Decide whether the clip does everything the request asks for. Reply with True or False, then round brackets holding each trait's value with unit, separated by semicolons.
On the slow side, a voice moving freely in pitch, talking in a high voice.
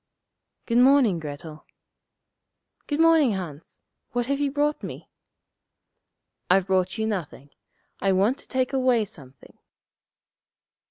True (120 wpm; 7.1 semitones; 220 Hz)